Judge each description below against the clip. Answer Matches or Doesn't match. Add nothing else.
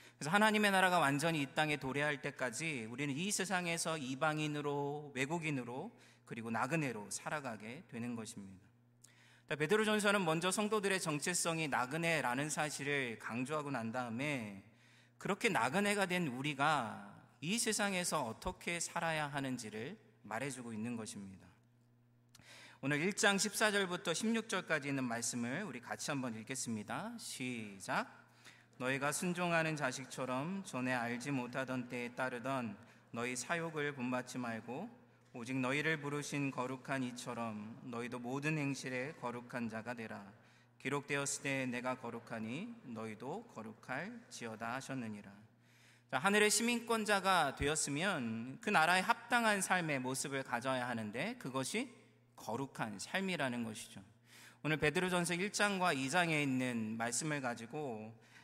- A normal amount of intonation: Doesn't match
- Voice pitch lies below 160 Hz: Matches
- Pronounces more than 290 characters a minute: Matches